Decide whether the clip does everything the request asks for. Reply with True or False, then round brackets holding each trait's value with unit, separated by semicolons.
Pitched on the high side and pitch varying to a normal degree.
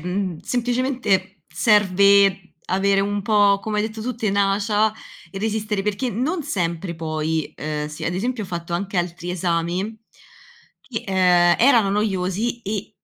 True (195 Hz; 3.4 semitones)